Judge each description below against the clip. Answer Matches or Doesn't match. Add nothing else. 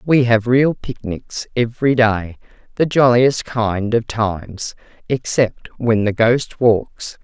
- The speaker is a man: Doesn't match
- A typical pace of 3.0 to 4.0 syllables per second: Matches